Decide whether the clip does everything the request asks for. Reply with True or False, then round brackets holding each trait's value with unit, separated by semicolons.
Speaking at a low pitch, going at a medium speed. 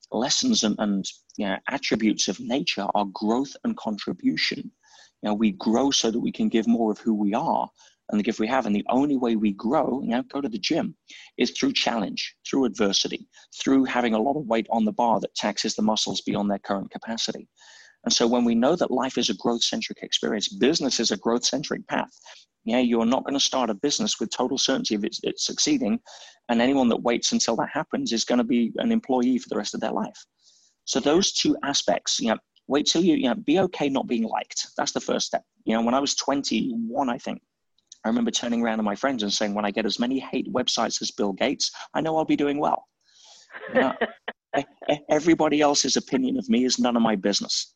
False (125 Hz; 230 wpm)